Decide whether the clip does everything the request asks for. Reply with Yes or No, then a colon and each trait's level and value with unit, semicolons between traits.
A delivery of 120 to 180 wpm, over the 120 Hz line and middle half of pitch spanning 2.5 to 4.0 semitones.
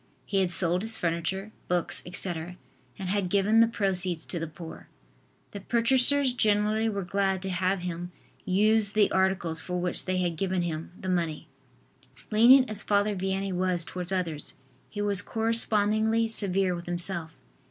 Yes: average, 160 wpm; high, 190 Hz; average, 3.1 semitones